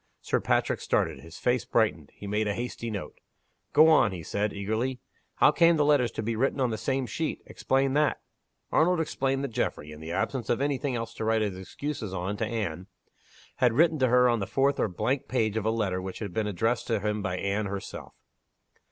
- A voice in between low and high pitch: No, low, 115 Hz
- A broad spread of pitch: No, average, 4.7 semitones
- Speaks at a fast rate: Yes, fast, 220 wpm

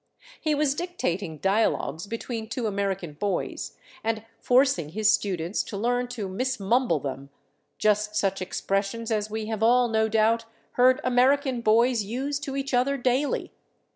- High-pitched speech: Yes, high, 220 Hz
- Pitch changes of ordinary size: Yes, average, 4.0 semitones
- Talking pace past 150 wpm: No, average, 145 wpm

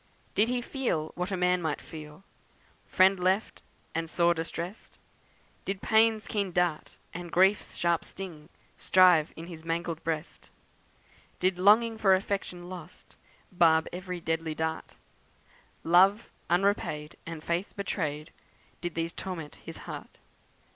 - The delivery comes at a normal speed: No, slow, 130 wpm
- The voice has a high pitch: No, medium, 175 Hz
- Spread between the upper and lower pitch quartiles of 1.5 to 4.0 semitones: Yes, average, 2.9 semitones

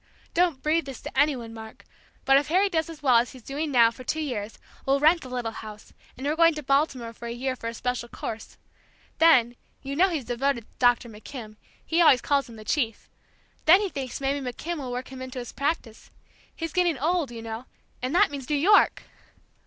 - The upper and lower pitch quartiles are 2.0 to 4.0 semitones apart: No, average, 4.5 semitones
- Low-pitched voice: No, very high, 270 Hz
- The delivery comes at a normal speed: No, fast, 220 wpm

